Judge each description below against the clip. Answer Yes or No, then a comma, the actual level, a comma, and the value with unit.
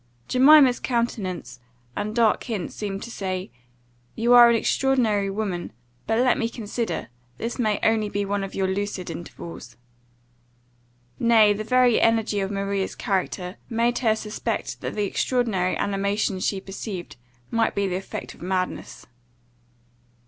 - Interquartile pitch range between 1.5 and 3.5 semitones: Yes, average, 3.2 semitones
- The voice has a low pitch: No, high, 210 Hz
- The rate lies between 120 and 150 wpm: Yes, average, 140 wpm